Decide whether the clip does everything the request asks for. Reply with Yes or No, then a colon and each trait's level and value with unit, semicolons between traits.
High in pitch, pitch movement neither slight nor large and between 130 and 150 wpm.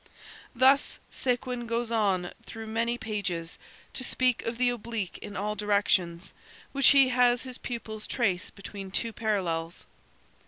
Yes: high, 225 Hz; average, 3.7 semitones; slow, 135 wpm